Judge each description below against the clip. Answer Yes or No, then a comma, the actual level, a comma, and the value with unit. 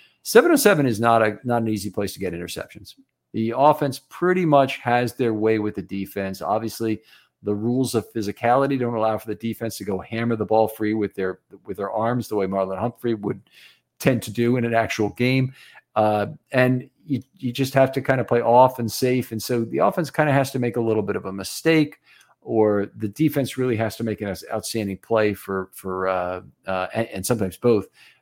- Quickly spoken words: Yes, fast, 215 wpm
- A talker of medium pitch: No, low, 115 Hz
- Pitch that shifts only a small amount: No, average, 3.6 semitones